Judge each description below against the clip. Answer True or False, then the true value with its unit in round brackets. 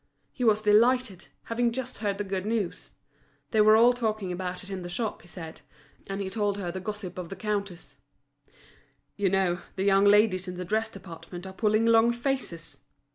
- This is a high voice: True (200 Hz)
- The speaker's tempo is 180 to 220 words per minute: True (190 wpm)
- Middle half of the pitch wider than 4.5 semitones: False (3.1 semitones)